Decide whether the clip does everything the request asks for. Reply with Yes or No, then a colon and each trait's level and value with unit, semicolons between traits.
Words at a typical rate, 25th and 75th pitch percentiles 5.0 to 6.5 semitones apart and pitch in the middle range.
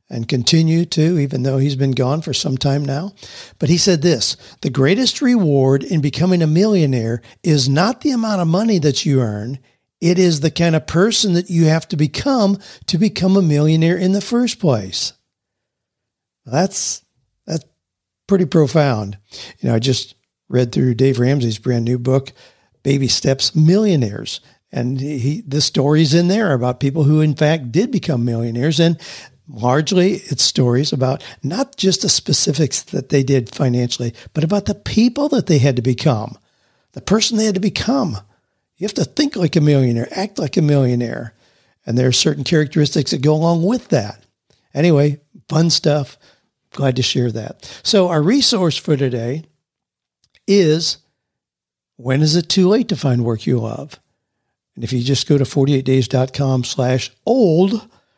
Yes: average, 170 wpm; wide, 5.5 semitones; medium, 150 Hz